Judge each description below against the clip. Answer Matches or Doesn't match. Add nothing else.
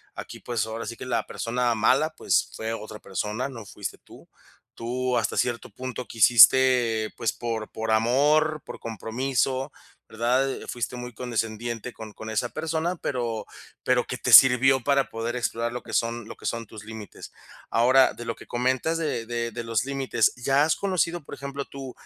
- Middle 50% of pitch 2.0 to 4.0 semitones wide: Matches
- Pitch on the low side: Matches